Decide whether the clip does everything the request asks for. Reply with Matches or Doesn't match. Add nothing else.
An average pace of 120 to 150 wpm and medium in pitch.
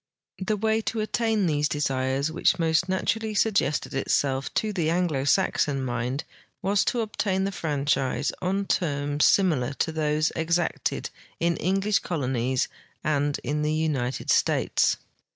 Matches